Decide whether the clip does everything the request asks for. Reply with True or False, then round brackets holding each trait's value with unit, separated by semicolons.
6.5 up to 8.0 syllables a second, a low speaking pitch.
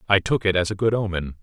True (6.6 syllables/s; 95 Hz)